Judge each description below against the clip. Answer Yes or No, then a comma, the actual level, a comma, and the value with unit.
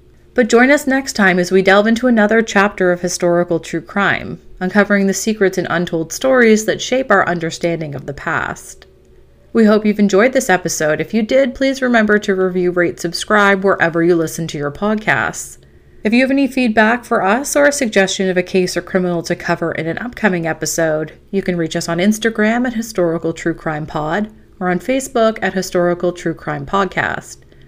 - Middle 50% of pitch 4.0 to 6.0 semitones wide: Yes, average, 4.6 semitones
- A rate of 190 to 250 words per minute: Yes, average, 195 wpm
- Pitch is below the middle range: No, high, 190 Hz